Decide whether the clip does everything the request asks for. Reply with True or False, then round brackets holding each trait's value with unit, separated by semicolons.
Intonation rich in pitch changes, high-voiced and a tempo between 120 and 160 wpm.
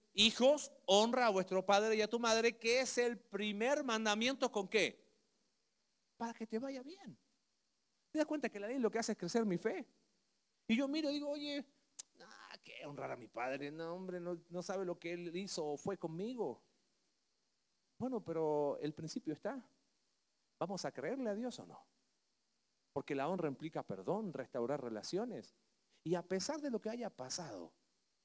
False (6.1 semitones; 215 Hz; 180 wpm)